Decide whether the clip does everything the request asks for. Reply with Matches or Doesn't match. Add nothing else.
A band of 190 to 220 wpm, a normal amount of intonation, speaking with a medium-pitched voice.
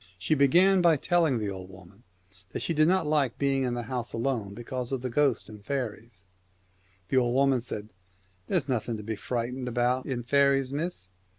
Doesn't match